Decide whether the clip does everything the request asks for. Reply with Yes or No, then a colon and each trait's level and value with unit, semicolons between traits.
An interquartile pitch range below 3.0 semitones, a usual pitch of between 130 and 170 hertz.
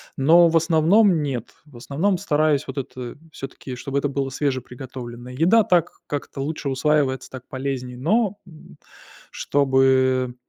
No: average, 3.4 semitones; medium, 140 Hz